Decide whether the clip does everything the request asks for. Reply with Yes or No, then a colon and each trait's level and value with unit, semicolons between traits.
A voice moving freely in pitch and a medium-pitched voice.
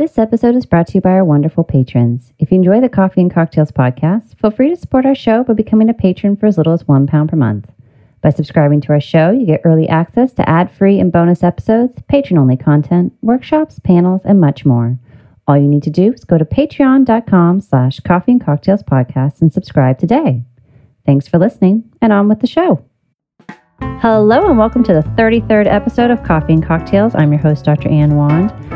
Yes: wide, 6.7 semitones; medium, 175 Hz